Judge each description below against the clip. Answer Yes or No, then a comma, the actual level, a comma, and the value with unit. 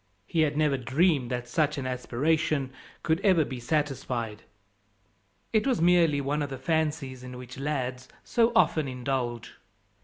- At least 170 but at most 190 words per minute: No, average, 150 wpm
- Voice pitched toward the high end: No, medium, 140 Hz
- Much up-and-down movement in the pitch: No, average, 3.8 semitones